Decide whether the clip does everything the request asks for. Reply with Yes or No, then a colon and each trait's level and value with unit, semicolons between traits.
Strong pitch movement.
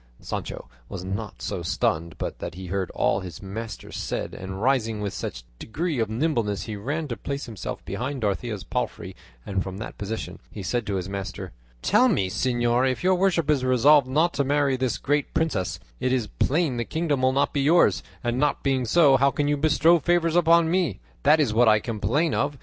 Yes: wide, 6.0 semitones